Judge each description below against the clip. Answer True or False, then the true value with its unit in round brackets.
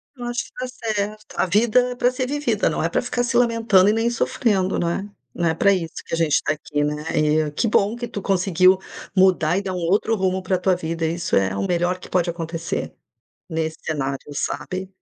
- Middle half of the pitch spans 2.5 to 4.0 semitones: False (5.1 semitones)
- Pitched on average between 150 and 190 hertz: True (185 Hz)